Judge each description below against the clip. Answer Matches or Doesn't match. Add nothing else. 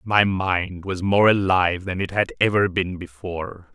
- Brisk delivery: Doesn't match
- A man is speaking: Matches